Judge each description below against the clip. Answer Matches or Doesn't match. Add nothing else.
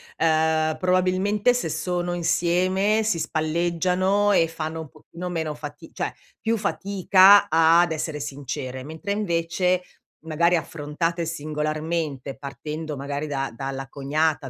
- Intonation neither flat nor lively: Matches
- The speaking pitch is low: Doesn't match